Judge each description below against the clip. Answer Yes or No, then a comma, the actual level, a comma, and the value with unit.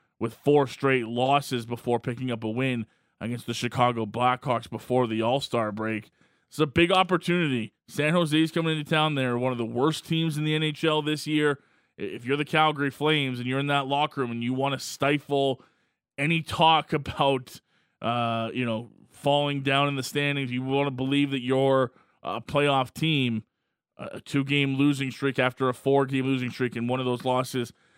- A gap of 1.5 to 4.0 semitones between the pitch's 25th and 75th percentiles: Yes, average, 2.8 semitones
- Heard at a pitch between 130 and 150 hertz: Yes, low, 135 Hz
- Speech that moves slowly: No, average, 185 wpm